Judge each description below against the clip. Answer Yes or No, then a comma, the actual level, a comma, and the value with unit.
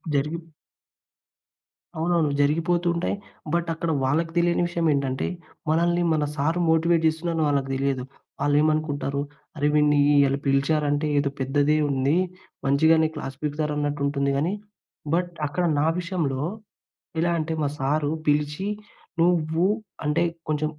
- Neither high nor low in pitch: Yes, medium, 150 Hz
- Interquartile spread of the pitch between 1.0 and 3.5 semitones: Yes, narrow, 2.6 semitones